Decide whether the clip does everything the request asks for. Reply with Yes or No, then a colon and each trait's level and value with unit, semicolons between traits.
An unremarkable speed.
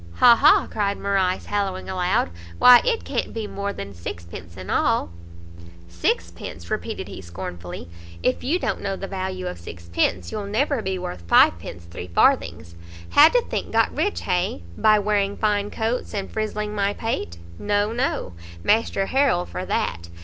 Yes: average, 160 wpm